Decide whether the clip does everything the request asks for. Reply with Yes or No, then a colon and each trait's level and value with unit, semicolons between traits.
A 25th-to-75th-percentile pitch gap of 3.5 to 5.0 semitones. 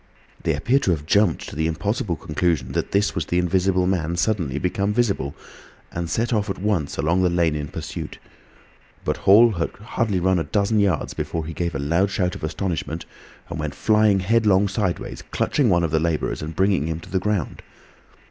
Yes: average, 3.9 semitones